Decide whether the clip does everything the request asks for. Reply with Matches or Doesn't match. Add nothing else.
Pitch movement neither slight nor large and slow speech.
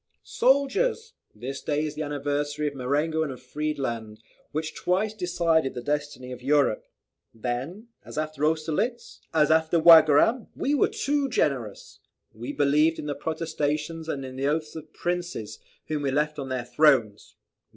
Doesn't match